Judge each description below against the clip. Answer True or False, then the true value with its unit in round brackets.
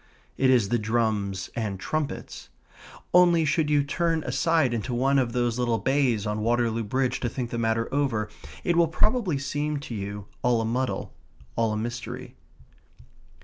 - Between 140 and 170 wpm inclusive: True (165 wpm)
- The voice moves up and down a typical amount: True (4.2 semitones)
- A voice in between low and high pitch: False (120 Hz)